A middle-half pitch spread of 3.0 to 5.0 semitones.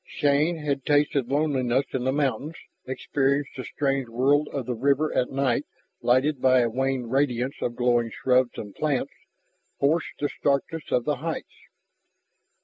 No: narrow, 2.5 semitones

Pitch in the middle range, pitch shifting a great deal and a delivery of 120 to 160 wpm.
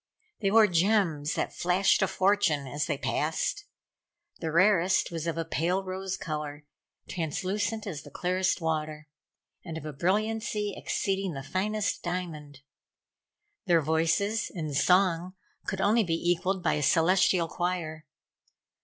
No: medium, 175 Hz; average, 3.5 semitones; slow, 135 wpm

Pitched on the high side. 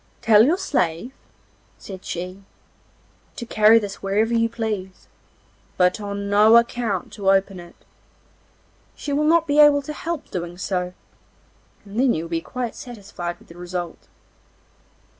Yes: high, 205 Hz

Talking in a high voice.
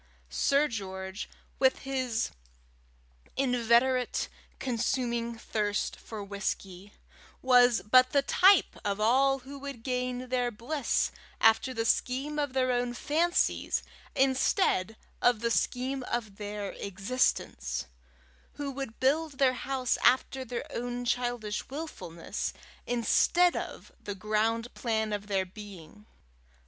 Yes: high, 245 Hz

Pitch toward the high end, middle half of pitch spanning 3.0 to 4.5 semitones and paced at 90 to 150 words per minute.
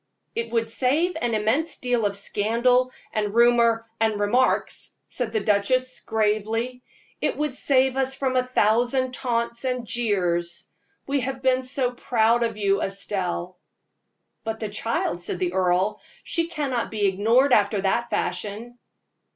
Yes: high, 230 Hz; average, 3.6 semitones; average, 145 wpm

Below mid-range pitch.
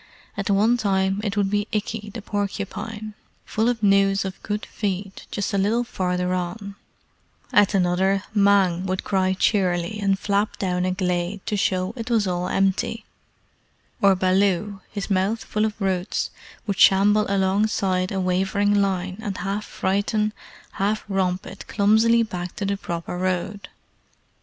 No: high, 195 Hz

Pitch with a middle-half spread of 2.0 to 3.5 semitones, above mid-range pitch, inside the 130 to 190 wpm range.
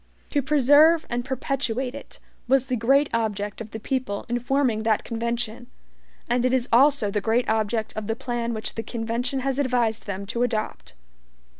Yes: average, 3.0 semitones; high, 240 Hz; average, 175 wpm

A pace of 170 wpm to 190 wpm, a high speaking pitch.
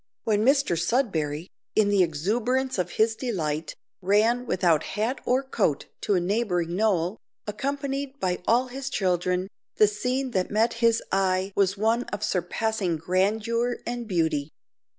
No: average, 145 wpm; high, 210 Hz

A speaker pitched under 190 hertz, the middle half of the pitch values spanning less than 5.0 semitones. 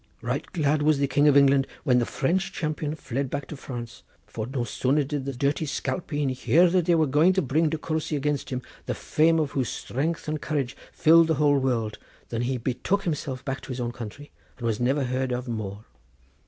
Yes: medium, 140 Hz; average, 3.4 semitones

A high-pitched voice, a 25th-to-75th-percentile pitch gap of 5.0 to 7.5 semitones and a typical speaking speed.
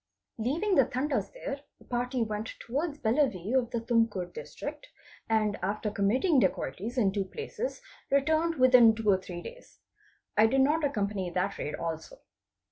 Yes: high, 235 Hz; wide, 5.4 semitones; average, 155 wpm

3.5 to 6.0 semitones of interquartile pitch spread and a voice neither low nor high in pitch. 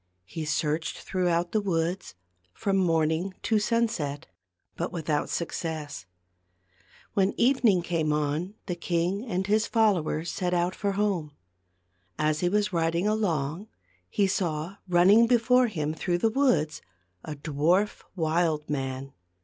Yes: average, 4.6 semitones; medium, 175 Hz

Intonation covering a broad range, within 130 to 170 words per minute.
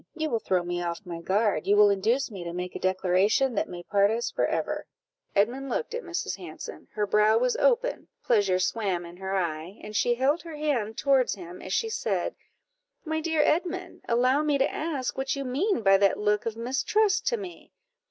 No: wide, 7.2 semitones; fast, 205 wpm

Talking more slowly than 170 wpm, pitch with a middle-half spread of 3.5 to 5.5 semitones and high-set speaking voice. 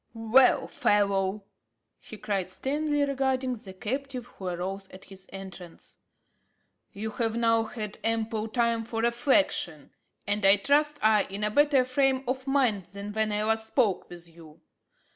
Yes: average, 150 wpm; average, 4.5 semitones; high, 220 Hz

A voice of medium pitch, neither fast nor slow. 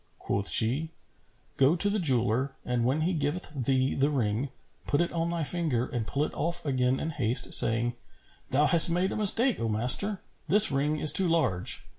Yes: medium, 145 Hz; average, 190 wpm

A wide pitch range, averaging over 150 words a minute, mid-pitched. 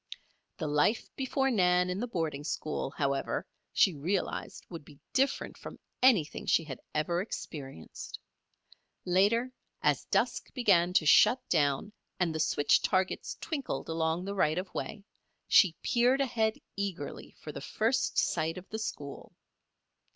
No: wide, 6.0 semitones; average, 145 wpm; medium, 180 Hz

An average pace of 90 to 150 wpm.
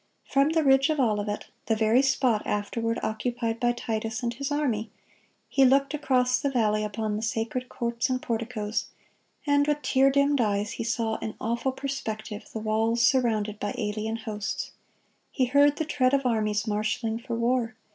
No: average, 170 wpm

